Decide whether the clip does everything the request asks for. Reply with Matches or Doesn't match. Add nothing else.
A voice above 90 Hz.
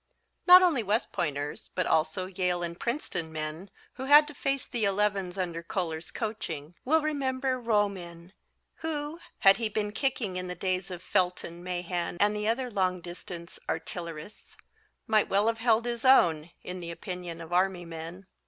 Matches